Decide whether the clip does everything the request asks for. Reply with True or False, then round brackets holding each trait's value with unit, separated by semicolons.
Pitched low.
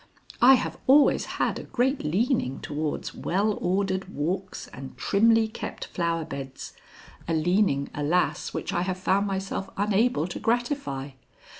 False (190 Hz)